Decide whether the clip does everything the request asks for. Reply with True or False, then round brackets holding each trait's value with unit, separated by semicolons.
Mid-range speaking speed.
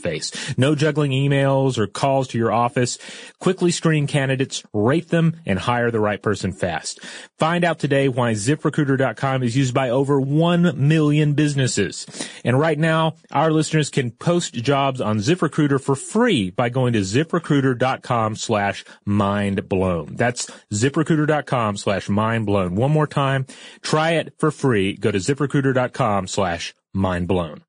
True (145 wpm)